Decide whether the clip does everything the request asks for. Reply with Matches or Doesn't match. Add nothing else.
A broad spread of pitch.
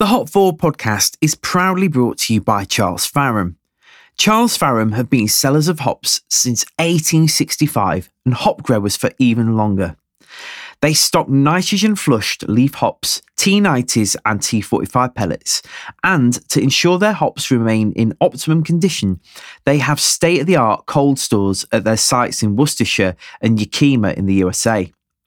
Matches